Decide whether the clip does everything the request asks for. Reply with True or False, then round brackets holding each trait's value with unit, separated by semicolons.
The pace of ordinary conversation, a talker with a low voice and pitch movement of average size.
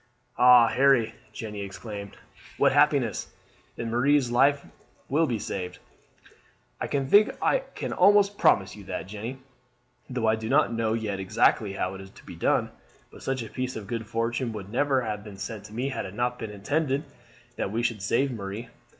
True (180 wpm; 115 Hz; 4.1 semitones)